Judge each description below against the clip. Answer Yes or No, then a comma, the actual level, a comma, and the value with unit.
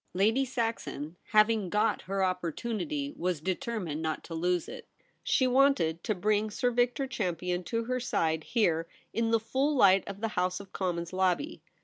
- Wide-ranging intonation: No, average, 4.9 semitones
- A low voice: No, high, 205 Hz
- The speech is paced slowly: No, average, 165 wpm